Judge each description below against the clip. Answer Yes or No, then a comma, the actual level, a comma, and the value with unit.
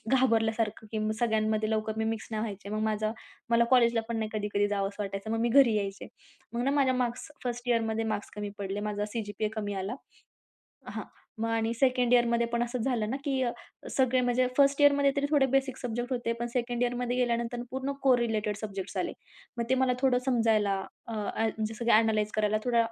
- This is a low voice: No, high, 230 Hz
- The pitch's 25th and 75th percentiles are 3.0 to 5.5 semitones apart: No, narrow, 2.5 semitones